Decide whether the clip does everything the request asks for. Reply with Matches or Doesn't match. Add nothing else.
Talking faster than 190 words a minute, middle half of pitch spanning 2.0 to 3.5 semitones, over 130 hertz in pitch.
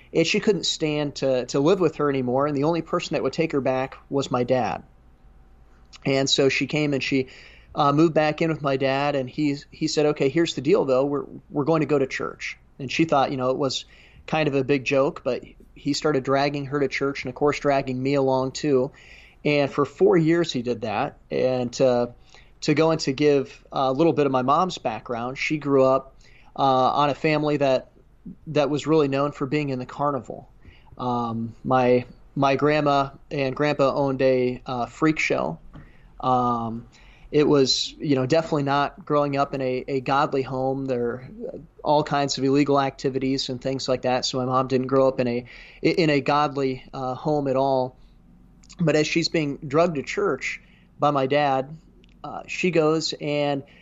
Matches